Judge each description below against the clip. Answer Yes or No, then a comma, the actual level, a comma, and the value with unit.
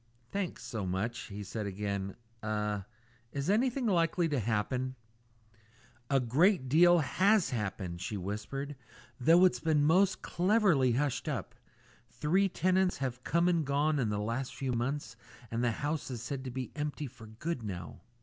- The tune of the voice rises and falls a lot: Yes, wide, 7.3 semitones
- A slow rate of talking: No, average, 160 wpm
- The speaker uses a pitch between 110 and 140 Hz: Yes, low, 135 Hz